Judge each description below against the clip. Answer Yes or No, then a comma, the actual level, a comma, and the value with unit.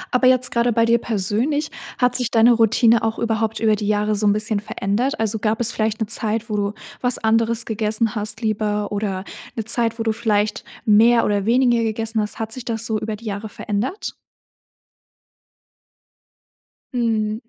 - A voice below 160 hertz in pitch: No, high, 225 Hz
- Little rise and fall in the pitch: Yes, narrow, 1.7 semitones